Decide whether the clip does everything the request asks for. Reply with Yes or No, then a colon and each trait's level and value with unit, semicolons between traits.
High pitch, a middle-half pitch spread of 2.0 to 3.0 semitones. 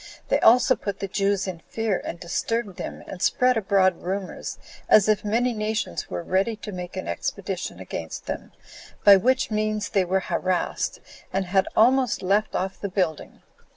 Yes: high, 200 Hz; average, 2.7 semitones